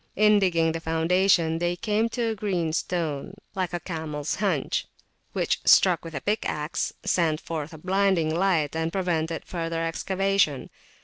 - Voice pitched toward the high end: No, medium, 170 Hz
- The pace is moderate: Yes, average, 145 wpm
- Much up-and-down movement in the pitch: No, average, 3.1 semitones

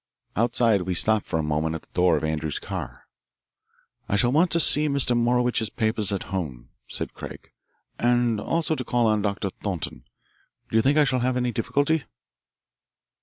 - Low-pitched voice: Yes, low, 110 Hz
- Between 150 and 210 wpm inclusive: Yes, average, 175 wpm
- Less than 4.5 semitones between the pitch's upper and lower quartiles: No, average, 5.3 semitones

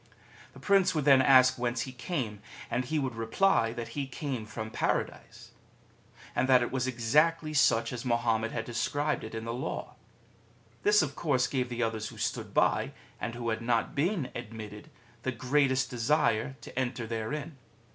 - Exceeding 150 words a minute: Yes, average, 175 wpm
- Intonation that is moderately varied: Yes, average, 3.4 semitones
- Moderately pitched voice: No, low, 125 Hz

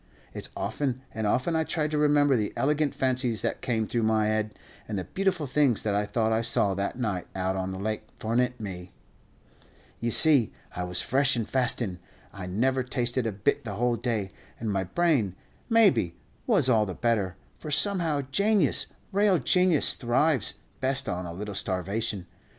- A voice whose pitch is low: Yes, low, 120 Hz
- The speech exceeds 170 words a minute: Yes, average, 180 wpm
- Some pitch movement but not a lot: No, wide, 5.7 semitones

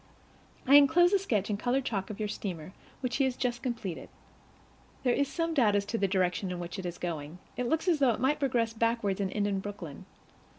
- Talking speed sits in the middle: No, fast, 225 wpm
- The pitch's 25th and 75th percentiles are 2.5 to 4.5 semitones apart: No, wide, 5.6 semitones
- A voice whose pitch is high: Yes, high, 220 Hz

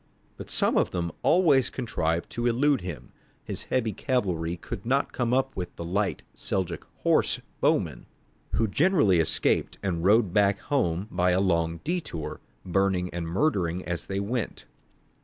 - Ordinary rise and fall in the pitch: No, wide, 6.0 semitones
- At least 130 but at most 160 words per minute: Yes, average, 155 wpm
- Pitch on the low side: Yes, very low, 95 Hz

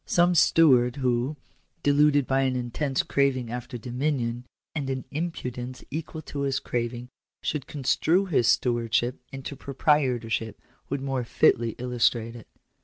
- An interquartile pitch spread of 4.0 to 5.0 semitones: No, average, 2.9 semitones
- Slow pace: Yes, slow, 130 wpm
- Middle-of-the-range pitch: No, low, 130 Hz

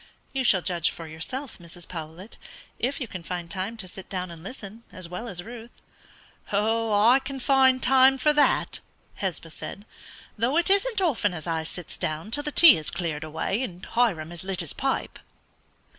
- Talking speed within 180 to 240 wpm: Yes, average, 185 wpm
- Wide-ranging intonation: Yes, wide, 7.1 semitones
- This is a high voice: Yes, high, 200 Hz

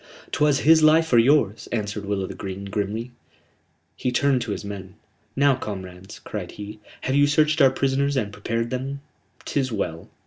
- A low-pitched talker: Yes, low, 120 Hz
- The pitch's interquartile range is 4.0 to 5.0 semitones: No, wide, 5.5 semitones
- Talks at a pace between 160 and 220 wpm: Yes, average, 175 wpm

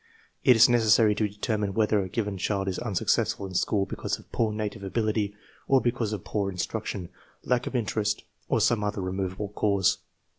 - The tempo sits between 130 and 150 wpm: No, average, 180 wpm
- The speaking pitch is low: Yes, low, 105 Hz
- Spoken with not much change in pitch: Yes, narrow, 2.2 semitones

